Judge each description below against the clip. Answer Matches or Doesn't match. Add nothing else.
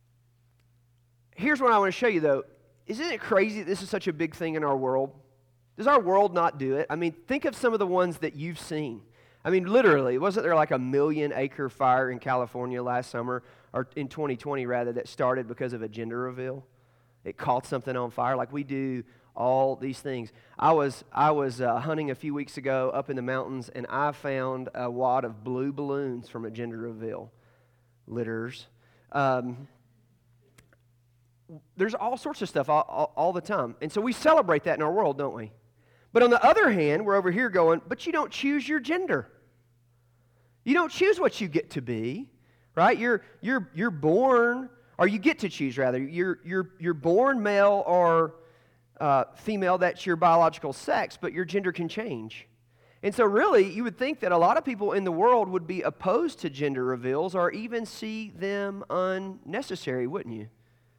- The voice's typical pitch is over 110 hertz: Matches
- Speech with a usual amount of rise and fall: Doesn't match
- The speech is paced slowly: Doesn't match